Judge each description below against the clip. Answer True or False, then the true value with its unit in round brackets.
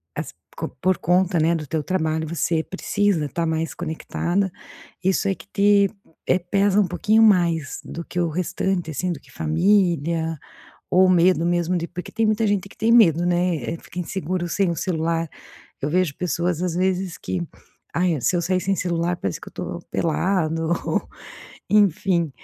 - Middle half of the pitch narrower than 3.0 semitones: True (2.4 semitones)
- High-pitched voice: False (175 Hz)